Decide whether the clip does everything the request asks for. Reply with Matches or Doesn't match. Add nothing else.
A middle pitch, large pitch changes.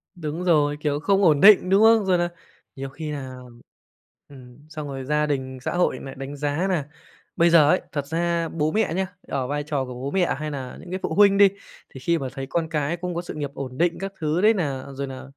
Doesn't match